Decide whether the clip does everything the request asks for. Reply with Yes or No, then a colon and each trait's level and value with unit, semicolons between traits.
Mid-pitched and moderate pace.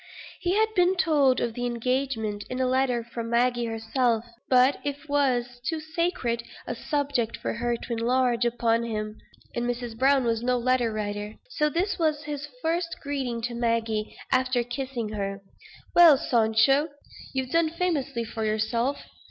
No: high, 245 Hz; average, 160 wpm